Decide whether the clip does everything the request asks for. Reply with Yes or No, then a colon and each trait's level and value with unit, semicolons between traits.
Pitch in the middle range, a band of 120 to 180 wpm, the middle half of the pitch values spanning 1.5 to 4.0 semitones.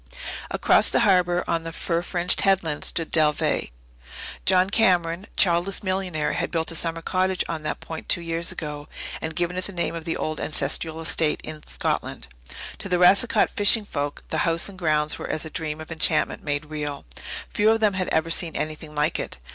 No: medium, 165 Hz; average, 195 wpm; average, 2.9 semitones